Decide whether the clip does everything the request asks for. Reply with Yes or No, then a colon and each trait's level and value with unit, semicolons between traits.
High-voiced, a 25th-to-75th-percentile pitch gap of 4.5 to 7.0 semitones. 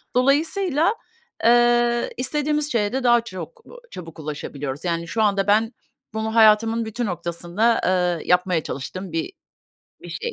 Yes: high, 220 Hz; wide, 5.4 semitones